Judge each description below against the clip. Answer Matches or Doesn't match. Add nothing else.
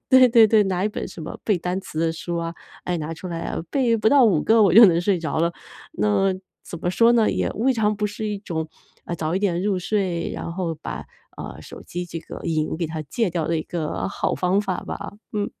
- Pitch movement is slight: Doesn't match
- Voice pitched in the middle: Matches